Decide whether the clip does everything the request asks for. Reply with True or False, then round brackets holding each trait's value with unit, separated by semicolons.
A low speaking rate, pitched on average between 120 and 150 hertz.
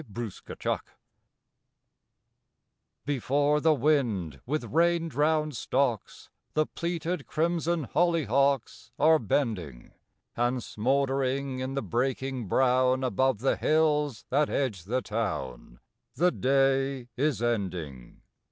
True (100 wpm; 135 Hz)